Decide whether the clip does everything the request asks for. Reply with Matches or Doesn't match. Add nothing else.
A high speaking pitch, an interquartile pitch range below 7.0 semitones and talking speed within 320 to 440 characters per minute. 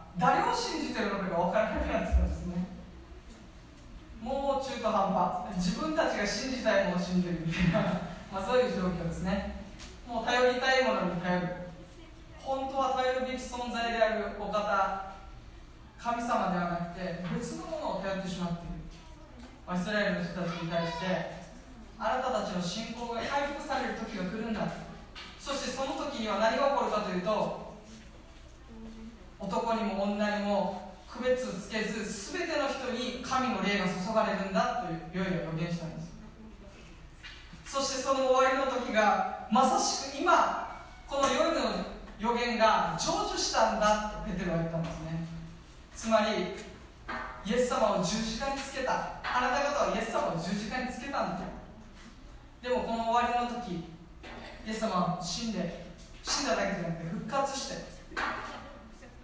Doesn't match